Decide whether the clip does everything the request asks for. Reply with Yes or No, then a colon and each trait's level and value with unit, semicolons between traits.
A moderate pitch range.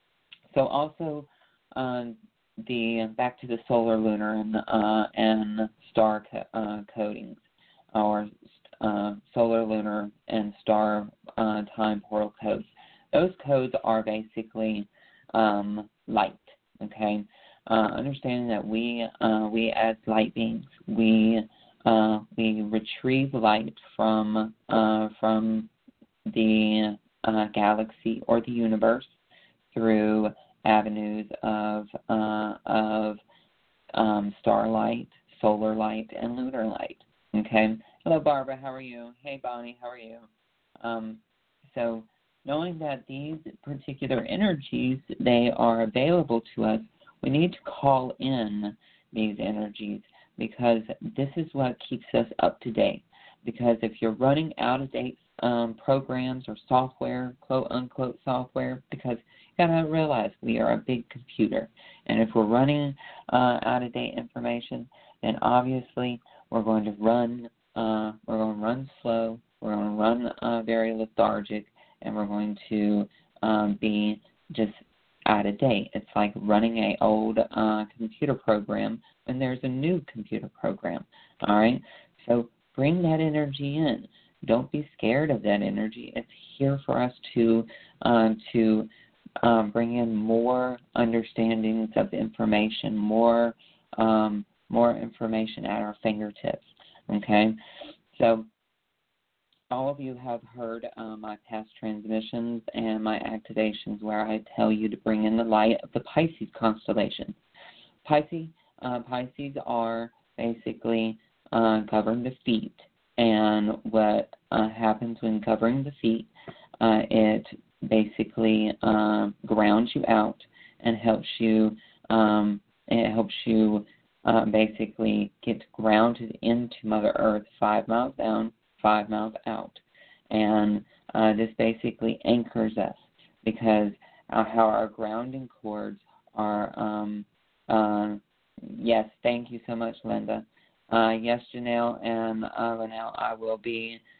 No: narrow, 1.9 semitones